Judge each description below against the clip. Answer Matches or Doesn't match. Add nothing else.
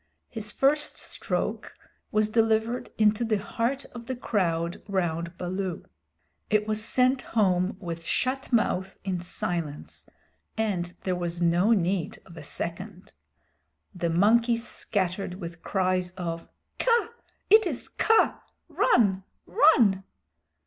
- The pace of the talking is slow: Matches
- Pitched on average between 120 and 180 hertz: Doesn't match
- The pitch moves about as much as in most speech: Matches